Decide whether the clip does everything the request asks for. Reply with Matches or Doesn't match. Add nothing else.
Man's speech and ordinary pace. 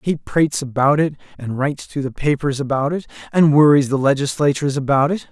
Matches